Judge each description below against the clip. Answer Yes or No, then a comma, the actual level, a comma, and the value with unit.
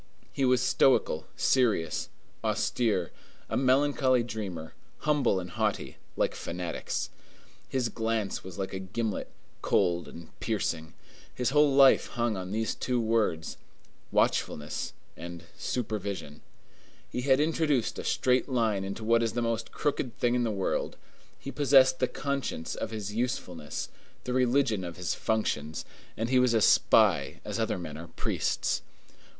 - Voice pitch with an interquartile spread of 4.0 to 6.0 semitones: Yes, wide, 5.5 semitones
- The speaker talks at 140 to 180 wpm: Yes, average, 145 wpm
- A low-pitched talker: Yes, low, 115 Hz